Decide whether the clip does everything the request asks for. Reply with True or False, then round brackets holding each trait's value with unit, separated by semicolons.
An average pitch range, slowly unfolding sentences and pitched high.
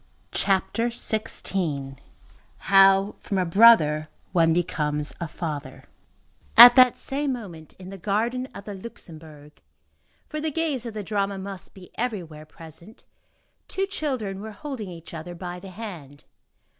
False (5.7 semitones; 130 wpm; 195 Hz)